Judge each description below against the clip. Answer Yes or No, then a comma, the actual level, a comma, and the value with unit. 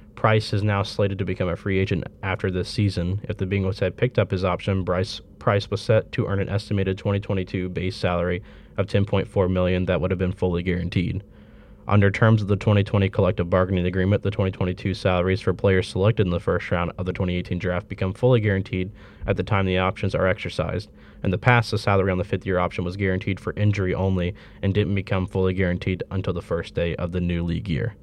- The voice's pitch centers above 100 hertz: No, very low, 95 Hz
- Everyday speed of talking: No, fast, 215 wpm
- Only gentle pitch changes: Yes, narrow, 1.9 semitones